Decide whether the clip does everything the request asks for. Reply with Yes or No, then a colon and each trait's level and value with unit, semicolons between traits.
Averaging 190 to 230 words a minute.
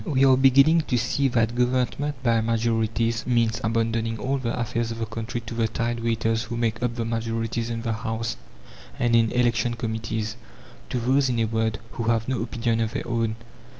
Yes: average, 195 wpm